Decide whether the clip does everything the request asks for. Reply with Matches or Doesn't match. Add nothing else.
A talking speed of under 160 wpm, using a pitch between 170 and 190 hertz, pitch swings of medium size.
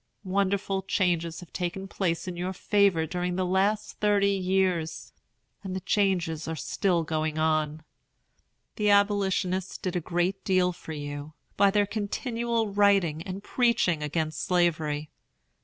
Matches